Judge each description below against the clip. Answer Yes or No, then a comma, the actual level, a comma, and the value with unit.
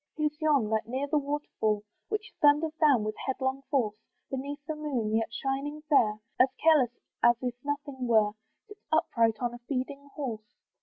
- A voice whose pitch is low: No, very high, 270 Hz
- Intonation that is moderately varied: Yes, average, 4.2 semitones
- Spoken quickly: No, average, 165 wpm